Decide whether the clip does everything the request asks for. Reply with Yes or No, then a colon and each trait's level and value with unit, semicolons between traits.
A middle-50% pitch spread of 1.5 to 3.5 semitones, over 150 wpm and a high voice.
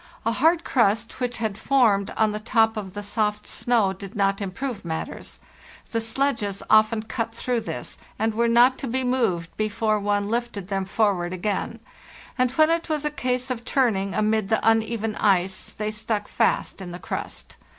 Yes: average, 3.0 semitones; average, 180 wpm; high, 220 Hz